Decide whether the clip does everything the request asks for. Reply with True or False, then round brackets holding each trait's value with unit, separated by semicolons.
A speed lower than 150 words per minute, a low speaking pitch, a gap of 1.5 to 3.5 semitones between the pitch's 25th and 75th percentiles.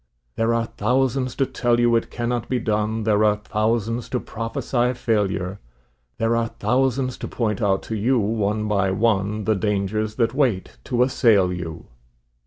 False (165 wpm; 110 Hz; 2.6 semitones)